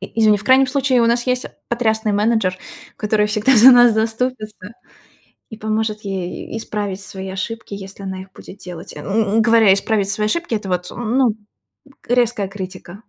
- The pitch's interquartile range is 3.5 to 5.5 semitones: No, average, 3.0 semitones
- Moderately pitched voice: No, high, 215 Hz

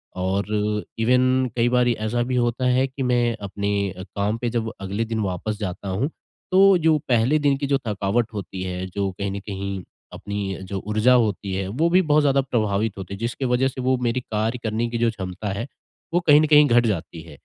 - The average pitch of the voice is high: No, low, 115 Hz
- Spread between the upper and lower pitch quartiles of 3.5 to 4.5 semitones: Yes, average, 4.2 semitones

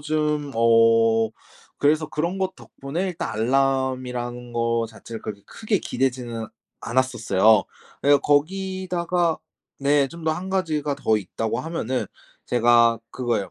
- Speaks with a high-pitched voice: No, low, 130 Hz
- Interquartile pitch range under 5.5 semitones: Yes, average, 5.1 semitones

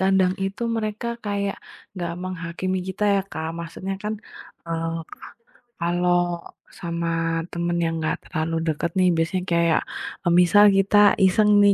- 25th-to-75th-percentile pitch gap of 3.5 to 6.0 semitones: No, narrow, 2.4 semitones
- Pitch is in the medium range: Yes, medium, 180 Hz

